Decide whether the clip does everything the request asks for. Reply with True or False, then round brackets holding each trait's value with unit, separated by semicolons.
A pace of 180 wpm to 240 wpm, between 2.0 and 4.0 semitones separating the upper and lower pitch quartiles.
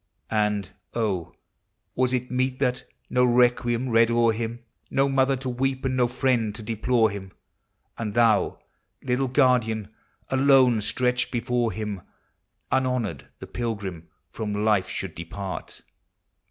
False (135 wpm; 3.1 semitones)